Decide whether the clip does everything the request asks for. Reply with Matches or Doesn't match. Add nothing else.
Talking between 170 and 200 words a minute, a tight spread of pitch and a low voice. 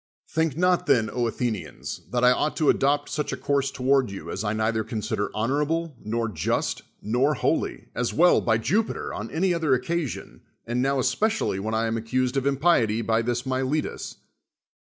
Doesn't match